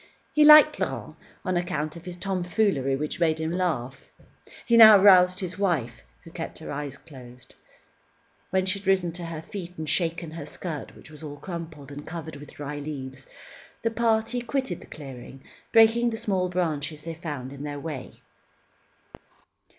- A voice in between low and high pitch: Yes, medium, 165 Hz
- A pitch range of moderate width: Yes, average, 4.6 semitones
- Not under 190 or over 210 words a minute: No, average, 170 wpm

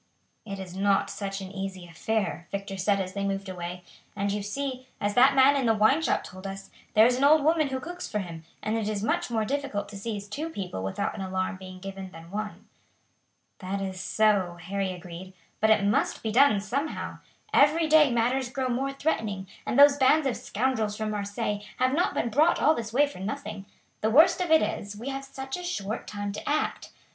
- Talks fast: Yes, fast, 215 wpm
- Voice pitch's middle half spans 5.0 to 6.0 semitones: Yes, wide, 5.5 semitones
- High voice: Yes, high, 215 Hz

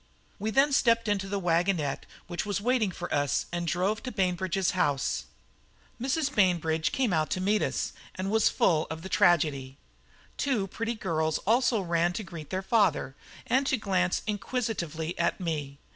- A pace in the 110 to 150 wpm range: No, average, 165 wpm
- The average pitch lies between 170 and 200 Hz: Yes, medium, 185 Hz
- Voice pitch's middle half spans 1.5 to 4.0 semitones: No, average, 4.6 semitones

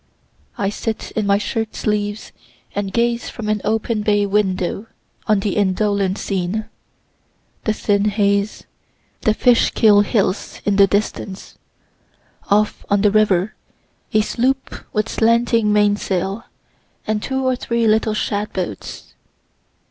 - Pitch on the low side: No, high, 210 Hz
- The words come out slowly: Yes, slow, 125 wpm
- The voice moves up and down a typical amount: No, narrow, 1.6 semitones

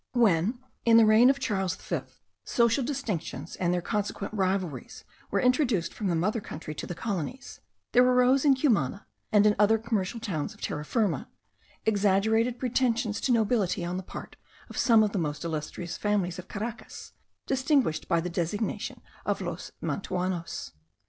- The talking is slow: No, average, 160 wpm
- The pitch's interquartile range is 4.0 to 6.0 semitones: Yes, average, 4.9 semitones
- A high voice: Yes, high, 210 Hz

